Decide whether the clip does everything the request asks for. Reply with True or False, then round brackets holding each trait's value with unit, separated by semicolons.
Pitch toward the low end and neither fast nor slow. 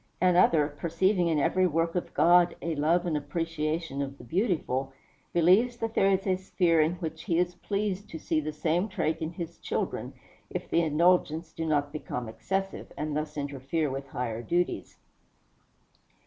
False (165 Hz; 170 wpm)